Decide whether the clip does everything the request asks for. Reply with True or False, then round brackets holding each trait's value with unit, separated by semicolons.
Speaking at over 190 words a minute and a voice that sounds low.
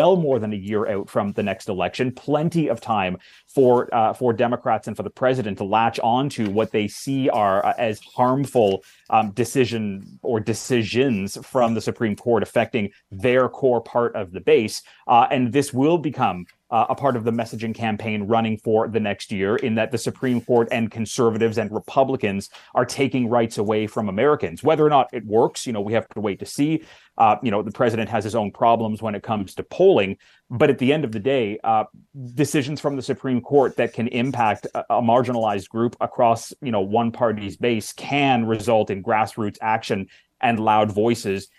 True (200 wpm; 115 Hz)